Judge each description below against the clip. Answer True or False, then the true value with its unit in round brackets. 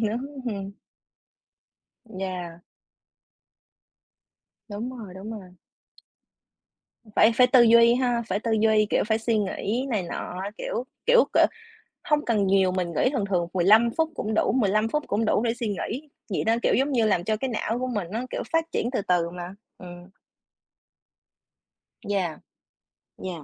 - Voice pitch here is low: False (220 Hz)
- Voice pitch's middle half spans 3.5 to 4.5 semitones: True (4.2 semitones)